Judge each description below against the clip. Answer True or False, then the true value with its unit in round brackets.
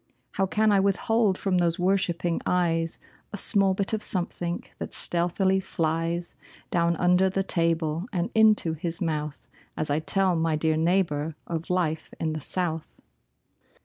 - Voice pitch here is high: False (175 Hz)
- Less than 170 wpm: True (150 wpm)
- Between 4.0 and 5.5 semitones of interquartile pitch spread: False (2.7 semitones)